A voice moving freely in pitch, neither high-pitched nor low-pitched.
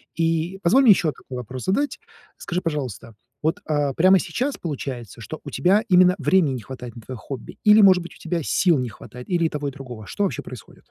Yes: wide, 6.0 semitones; medium, 160 Hz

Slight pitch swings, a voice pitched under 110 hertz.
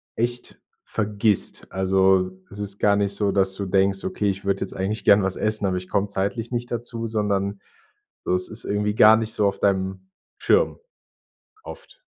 Yes: narrow, 1.9 semitones; low, 100 Hz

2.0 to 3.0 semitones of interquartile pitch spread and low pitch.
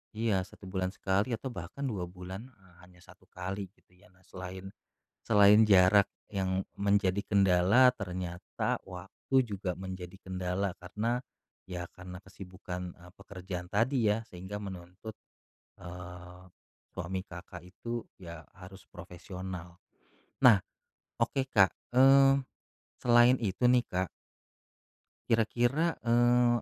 No: average, 3.6 semitones; very low, 95 Hz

